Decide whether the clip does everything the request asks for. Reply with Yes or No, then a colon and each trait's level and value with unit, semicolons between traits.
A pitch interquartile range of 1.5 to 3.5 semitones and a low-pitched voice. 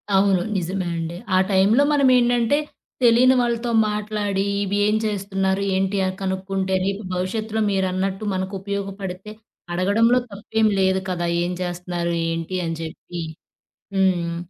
No: narrow, 2.4 semitones; high, 195 Hz